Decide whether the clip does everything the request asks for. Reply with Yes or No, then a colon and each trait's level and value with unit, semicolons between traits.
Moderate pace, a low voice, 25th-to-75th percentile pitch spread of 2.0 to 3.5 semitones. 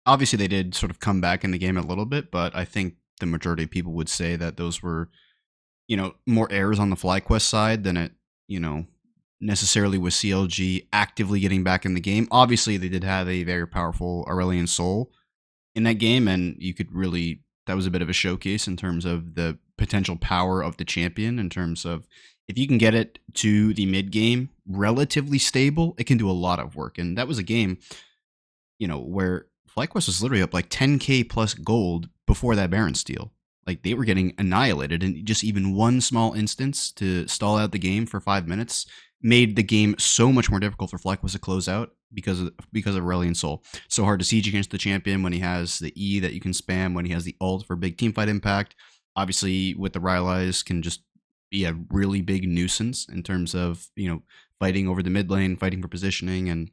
No: fast, 220 wpm; very low, 95 Hz; average, 3.2 semitones